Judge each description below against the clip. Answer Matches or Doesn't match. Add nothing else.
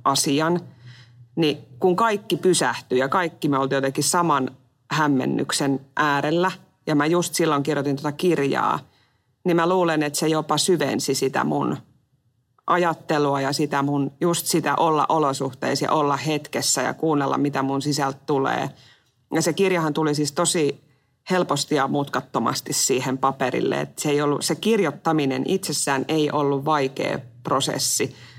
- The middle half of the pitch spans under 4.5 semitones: Matches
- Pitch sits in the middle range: Matches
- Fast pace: Doesn't match